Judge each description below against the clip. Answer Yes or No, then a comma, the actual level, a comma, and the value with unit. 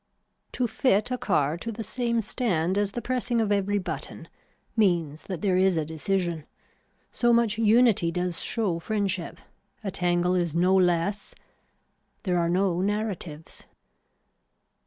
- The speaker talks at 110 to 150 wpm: Yes, average, 140 wpm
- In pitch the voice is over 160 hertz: Yes, high, 190 Hz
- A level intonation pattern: No, average, 4.0 semitones